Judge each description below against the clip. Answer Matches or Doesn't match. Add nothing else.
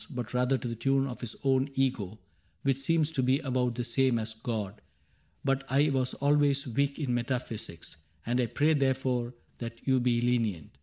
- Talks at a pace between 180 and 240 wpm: Matches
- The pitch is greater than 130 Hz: Doesn't match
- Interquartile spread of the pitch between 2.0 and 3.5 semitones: Matches